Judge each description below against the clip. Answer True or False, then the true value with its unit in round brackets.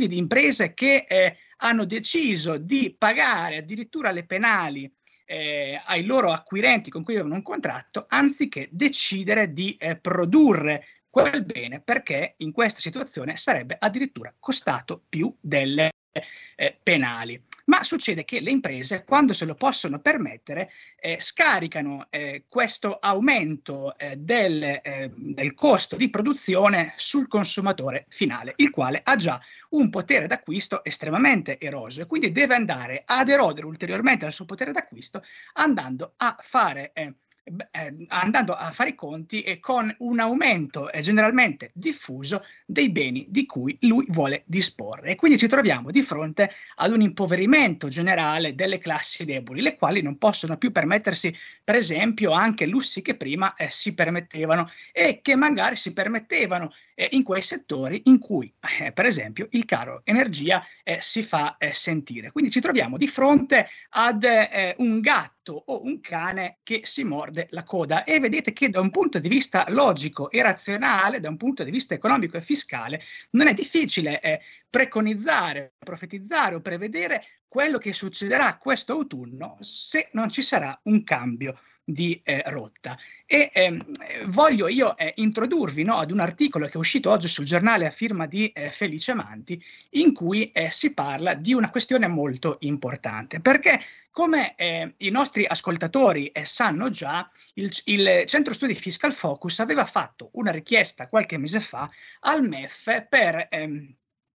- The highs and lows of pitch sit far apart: True (8.3 semitones)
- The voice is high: True (200 Hz)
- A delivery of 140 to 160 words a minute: True (155 wpm)